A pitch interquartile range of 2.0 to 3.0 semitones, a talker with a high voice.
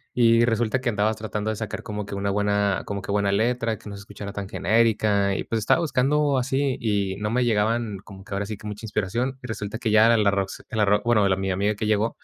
No: narrow, 2.4 semitones; low, 105 Hz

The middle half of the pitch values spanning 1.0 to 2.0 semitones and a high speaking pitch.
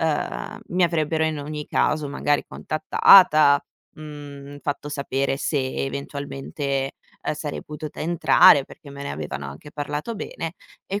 No: narrow, 1.7 semitones; medium, 145 Hz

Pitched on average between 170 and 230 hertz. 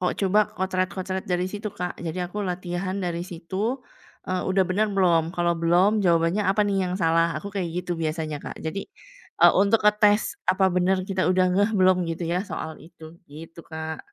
Yes: medium, 185 Hz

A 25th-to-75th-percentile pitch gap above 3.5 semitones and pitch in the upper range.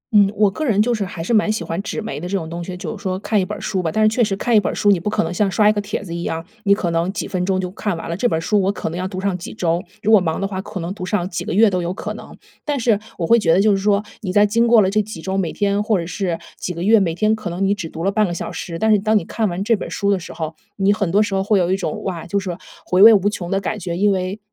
No: average, 2.9 semitones; high, 195 Hz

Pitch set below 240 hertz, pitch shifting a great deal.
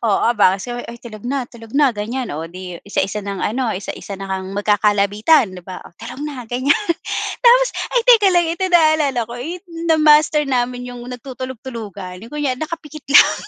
No: high, 245 Hz; wide, 6.4 semitones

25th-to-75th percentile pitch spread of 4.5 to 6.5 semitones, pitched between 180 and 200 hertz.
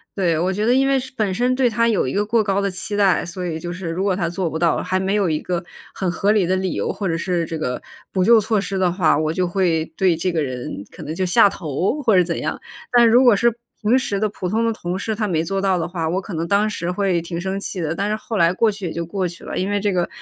No: average, 3.4 semitones; high, 190 Hz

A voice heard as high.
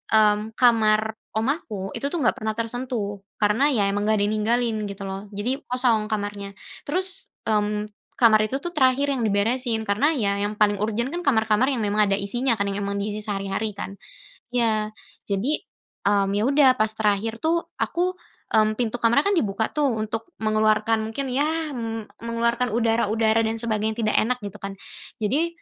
Yes: high, 220 Hz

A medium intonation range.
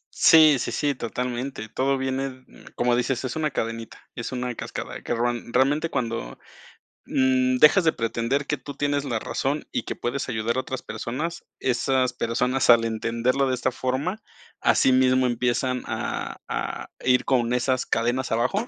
No: narrow, 2.2 semitones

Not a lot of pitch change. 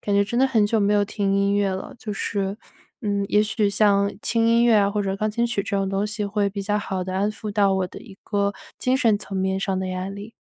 Yes: narrow, 1.4 semitones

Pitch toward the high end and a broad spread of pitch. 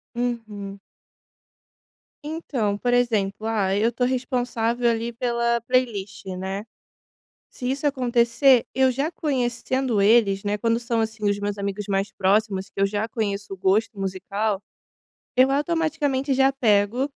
No: high, 230 Hz; average, 3.8 semitones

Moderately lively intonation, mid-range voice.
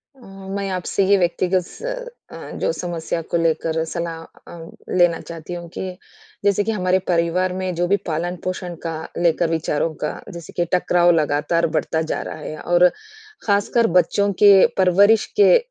No: narrow, 2.3 semitones; medium, 175 Hz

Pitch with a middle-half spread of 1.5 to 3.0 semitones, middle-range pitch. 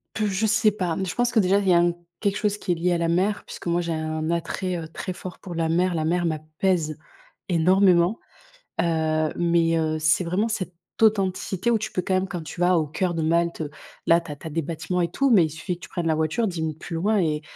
Yes: average, 2.7 semitones; medium, 175 Hz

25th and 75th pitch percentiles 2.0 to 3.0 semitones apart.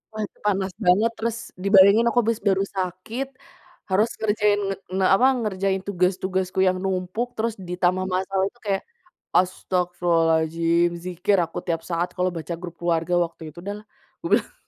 Yes: narrow, 2.6 semitones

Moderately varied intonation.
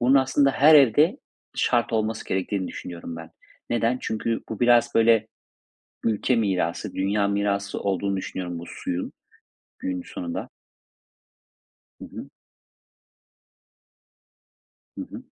Yes: average, 4.0 semitones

